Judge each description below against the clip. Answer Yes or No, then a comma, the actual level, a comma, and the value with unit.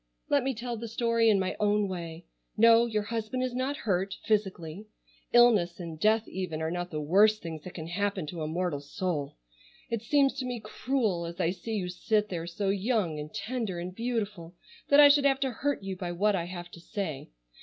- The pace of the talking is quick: Yes, fast, 210 wpm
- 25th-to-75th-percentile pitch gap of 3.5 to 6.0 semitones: Yes, average, 4.9 semitones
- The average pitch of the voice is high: Yes, high, 200 Hz